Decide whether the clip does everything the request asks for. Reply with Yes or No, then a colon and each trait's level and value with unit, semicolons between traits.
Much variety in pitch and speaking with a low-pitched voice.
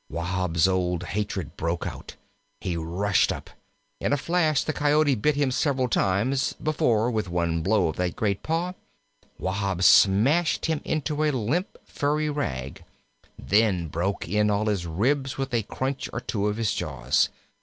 Yes: wide, 7.8 semitones; low, 105 Hz